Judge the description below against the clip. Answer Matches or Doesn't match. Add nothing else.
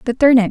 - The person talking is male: Doesn't match